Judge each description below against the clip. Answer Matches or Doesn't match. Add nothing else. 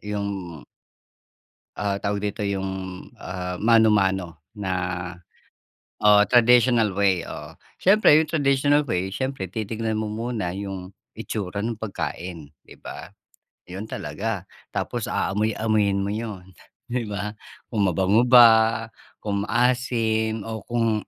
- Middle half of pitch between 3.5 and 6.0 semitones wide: Doesn't match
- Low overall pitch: Matches